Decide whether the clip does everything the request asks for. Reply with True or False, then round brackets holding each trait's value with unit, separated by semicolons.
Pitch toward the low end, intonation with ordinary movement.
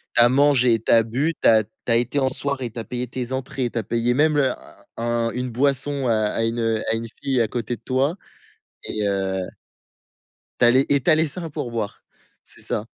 True (125 Hz; 3.1 semitones)